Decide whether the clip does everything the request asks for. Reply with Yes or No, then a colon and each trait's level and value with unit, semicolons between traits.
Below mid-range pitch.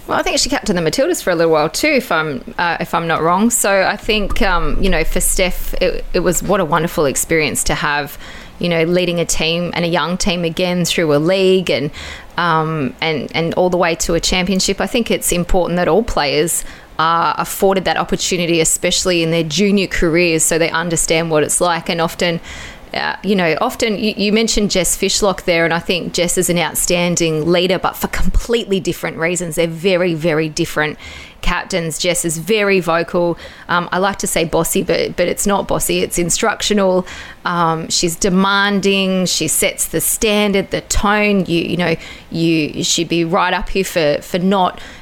No: medium, 175 Hz